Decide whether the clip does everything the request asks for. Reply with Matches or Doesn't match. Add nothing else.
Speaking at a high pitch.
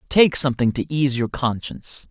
Doesn't match